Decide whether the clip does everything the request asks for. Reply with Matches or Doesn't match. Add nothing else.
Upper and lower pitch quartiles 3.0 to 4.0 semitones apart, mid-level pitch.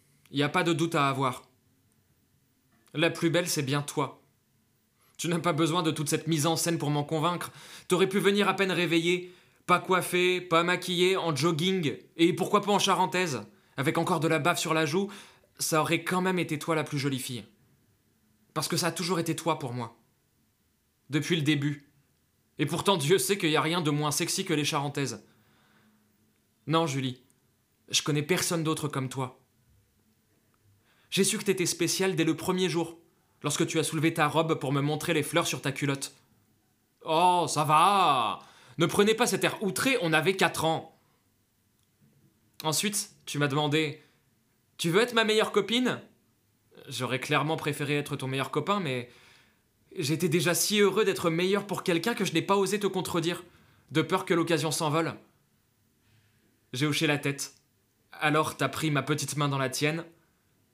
Doesn't match